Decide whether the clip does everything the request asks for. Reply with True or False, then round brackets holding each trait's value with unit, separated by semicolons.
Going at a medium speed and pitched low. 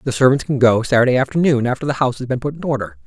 False (275 wpm; 130 Hz)